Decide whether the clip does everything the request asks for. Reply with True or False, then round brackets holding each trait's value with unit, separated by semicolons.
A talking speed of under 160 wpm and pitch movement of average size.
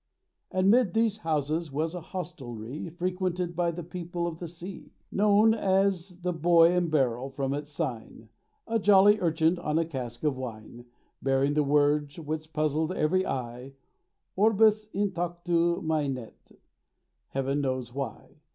True (145 wpm; 4.5 semitones)